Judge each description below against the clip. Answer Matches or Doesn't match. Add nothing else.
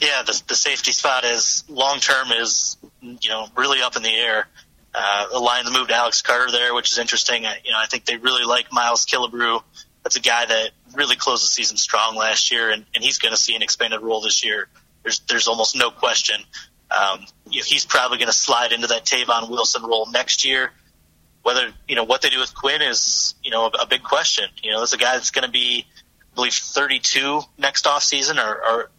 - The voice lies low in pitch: Matches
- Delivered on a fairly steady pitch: Matches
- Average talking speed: Doesn't match